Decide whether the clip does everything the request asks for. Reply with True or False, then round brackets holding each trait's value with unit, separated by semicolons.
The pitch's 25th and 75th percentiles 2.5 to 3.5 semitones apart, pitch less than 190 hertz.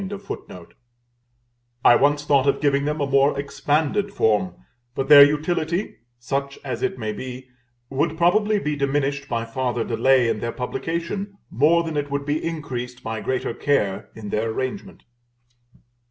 False (4.1 semitones; 140 Hz)